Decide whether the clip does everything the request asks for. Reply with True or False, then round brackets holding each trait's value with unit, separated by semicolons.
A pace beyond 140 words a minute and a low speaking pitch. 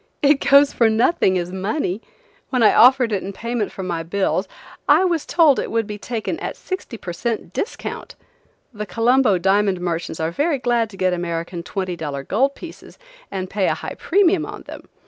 False (190 wpm; 210 Hz)